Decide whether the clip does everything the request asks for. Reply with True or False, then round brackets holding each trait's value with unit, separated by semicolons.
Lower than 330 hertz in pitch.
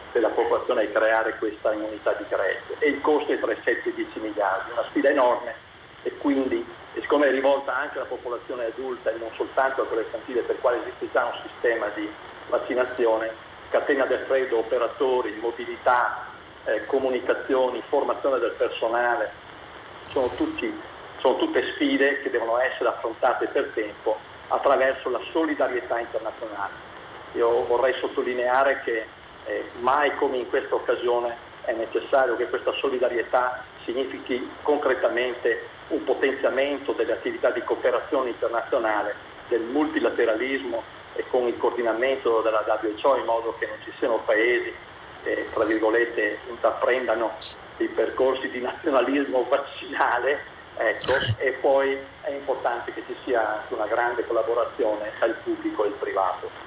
False (390 Hz)